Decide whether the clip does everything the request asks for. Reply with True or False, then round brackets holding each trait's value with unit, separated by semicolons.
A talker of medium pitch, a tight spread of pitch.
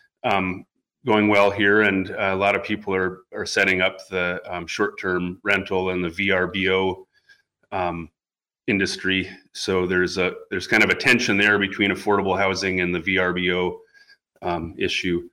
False (95 Hz; 1.9 semitones)